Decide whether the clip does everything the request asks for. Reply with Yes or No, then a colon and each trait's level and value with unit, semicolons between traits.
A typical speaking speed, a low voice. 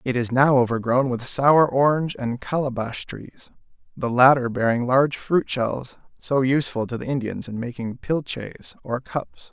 Yes: average, 165 wpm; low, 130 Hz